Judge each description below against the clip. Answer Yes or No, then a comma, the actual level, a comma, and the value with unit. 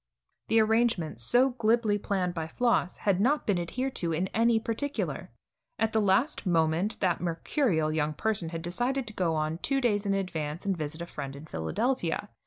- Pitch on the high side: Yes, high, 195 Hz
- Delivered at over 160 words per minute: Yes, average, 185 wpm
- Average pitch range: No, wide, 5.7 semitones